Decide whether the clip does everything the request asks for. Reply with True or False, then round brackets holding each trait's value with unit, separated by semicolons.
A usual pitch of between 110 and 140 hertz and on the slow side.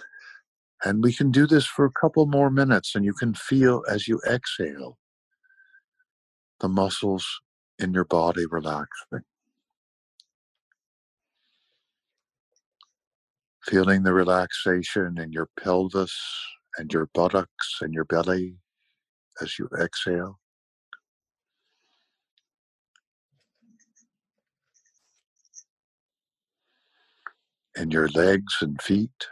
False (100 Hz; 90 wpm)